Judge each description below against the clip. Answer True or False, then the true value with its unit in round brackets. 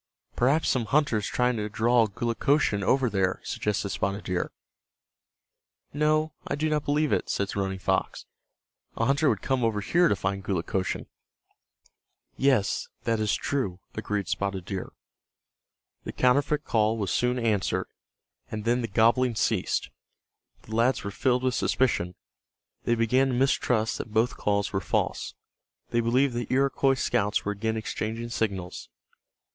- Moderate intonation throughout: True (4.1 semitones)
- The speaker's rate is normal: True (150 wpm)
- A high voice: False (115 Hz)